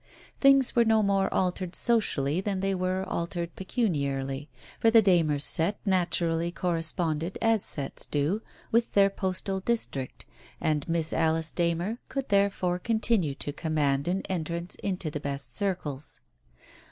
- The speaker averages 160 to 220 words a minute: No, average, 140 wpm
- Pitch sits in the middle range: Yes, medium, 175 Hz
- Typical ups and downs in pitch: Yes, average, 4.1 semitones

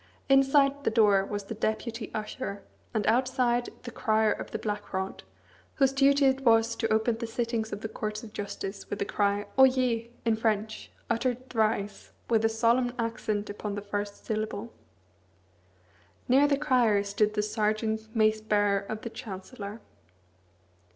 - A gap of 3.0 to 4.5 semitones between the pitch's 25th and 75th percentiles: No, narrow, 2.5 semitones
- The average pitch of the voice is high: Yes, high, 220 Hz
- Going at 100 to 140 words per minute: No, average, 155 wpm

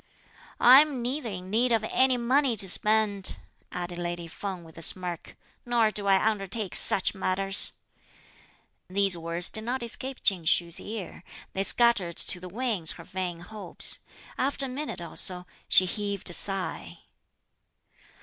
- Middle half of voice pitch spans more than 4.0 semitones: Yes, average, 4.7 semitones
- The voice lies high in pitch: Yes, high, 195 Hz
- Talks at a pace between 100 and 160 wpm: Yes, average, 150 wpm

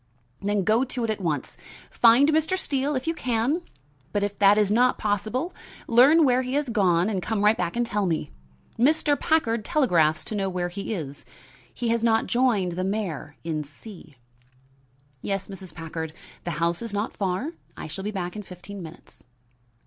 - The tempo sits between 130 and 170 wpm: No, average, 185 wpm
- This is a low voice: No, high, 205 Hz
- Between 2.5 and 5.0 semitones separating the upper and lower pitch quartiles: No, wide, 5.4 semitones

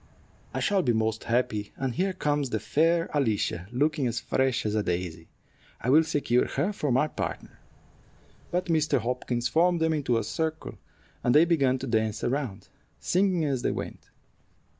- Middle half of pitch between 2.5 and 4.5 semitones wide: No, wide, 5.6 semitones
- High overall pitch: No, low, 130 Hz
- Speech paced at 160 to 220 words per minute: Yes, average, 170 wpm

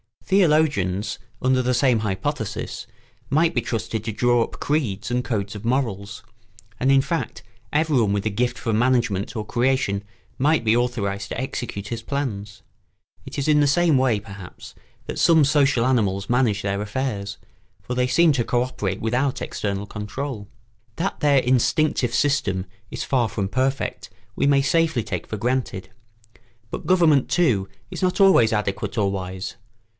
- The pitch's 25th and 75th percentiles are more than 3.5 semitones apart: Yes, average, 5.1 semitones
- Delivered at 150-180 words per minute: Yes, average, 160 wpm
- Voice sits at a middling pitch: No, low, 120 Hz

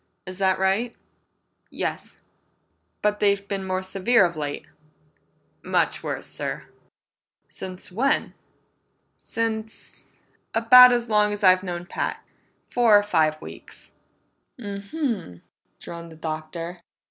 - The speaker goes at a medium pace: No, slow, 115 wpm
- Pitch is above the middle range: Yes, high, 195 Hz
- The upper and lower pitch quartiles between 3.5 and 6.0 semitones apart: Yes, average, 3.9 semitones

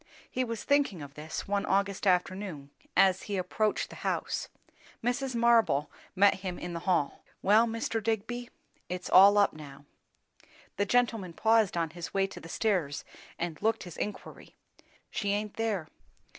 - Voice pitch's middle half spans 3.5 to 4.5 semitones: Yes, average, 4.2 semitones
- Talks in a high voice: Yes, high, 200 Hz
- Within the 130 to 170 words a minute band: Yes, average, 155 wpm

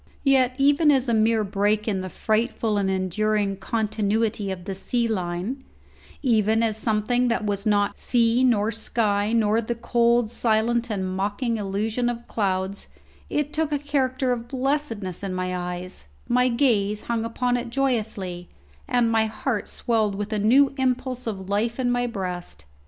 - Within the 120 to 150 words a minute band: No, average, 165 wpm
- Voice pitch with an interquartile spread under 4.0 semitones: Yes, average, 3.3 semitones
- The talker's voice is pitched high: Yes, high, 220 Hz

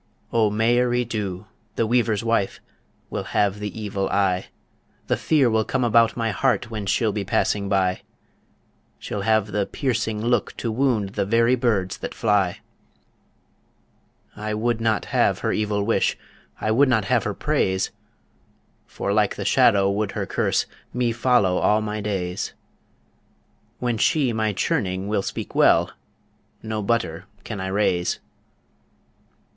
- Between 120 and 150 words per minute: Yes, average, 145 wpm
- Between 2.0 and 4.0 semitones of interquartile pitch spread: Yes, average, 2.7 semitones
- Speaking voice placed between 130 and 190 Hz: No, low, 105 Hz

